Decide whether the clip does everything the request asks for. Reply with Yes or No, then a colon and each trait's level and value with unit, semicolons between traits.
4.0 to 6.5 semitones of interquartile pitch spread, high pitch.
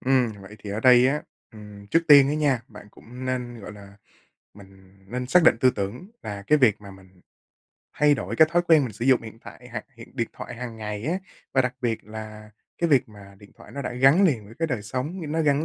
No: average, 4.8 semitones; low, 120 Hz